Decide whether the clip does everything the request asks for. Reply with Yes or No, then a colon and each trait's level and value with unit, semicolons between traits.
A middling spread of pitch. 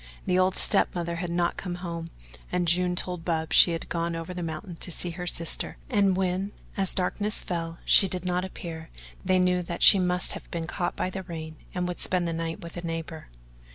No: narrow, 1.5 semitones